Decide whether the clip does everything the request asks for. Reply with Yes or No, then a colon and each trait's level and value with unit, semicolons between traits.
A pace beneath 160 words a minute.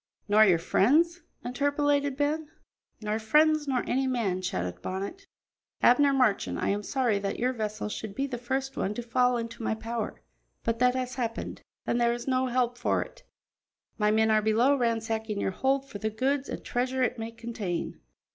No: average, 185 wpm